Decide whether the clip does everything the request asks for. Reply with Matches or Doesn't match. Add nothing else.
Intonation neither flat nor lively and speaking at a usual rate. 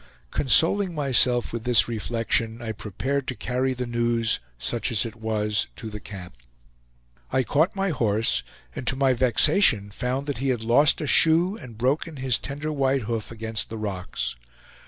Matches